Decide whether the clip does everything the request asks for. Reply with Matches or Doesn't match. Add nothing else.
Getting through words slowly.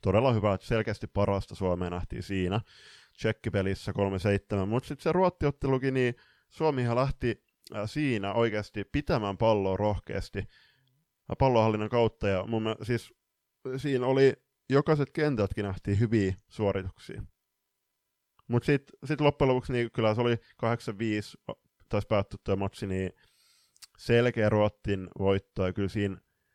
Doesn't match